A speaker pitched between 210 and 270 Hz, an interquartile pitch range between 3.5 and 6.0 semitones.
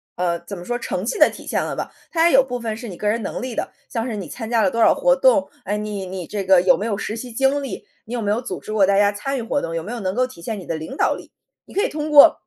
Yes: high, 220 Hz; average, 4.6 semitones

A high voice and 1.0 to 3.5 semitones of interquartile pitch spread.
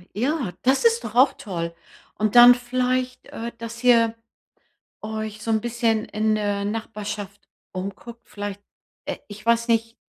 Yes: high, 225 Hz; narrow, 2.5 semitones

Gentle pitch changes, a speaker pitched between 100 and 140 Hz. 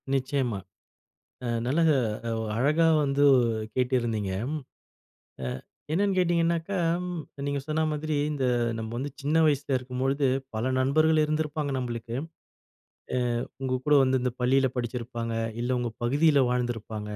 No: average, 3.7 semitones; low, 135 Hz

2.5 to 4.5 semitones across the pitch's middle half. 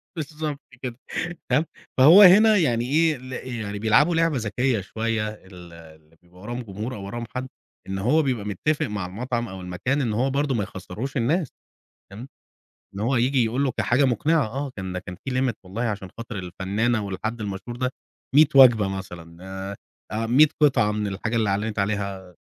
No: average, 5.1 semitones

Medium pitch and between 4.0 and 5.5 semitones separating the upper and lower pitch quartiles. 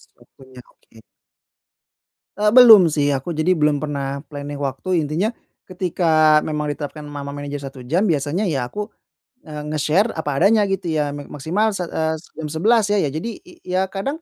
Yes: medium, 155 Hz; average, 4.6 semitones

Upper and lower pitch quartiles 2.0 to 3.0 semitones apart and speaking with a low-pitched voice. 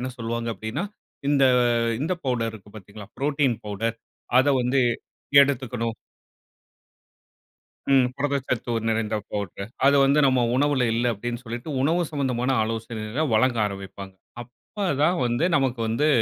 No: average, 3.7 semitones; low, 120 Hz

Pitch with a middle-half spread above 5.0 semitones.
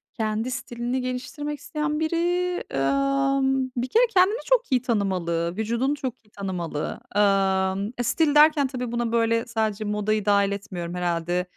Yes: wide, 5.6 semitones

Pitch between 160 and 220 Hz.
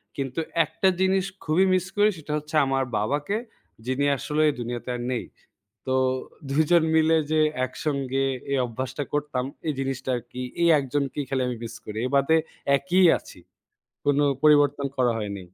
No: medium, 140 Hz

